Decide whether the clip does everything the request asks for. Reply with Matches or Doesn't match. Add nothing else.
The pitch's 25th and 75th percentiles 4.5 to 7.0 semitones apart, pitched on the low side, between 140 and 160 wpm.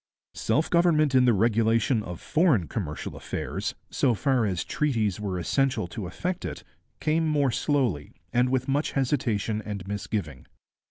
Matches